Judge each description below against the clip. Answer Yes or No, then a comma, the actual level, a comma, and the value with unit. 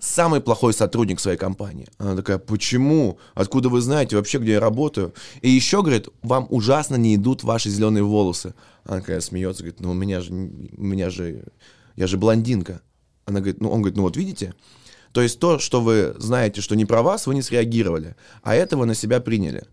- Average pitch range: Yes, average, 4.8 semitones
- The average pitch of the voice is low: Yes, low, 110 Hz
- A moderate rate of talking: No, fast, 200 wpm